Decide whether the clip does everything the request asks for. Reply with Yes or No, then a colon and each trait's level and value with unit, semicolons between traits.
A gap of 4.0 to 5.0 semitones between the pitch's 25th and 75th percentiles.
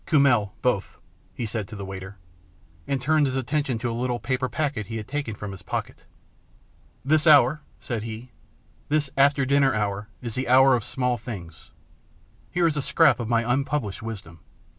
Yes: average, 4.3 semitones